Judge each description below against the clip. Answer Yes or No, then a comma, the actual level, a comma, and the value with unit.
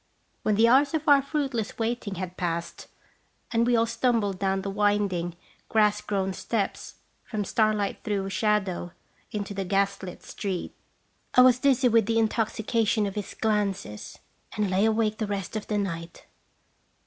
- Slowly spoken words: No, average, 160 wpm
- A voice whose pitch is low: No, high, 210 Hz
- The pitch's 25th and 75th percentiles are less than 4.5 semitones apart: Yes, average, 2.8 semitones